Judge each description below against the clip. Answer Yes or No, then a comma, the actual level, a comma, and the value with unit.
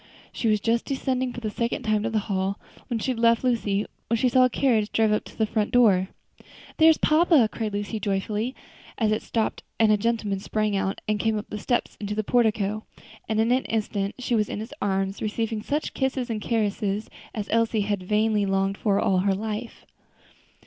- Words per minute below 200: No, fast, 205 wpm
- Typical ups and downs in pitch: No, narrow, 2.2 semitones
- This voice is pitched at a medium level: No, high, 215 Hz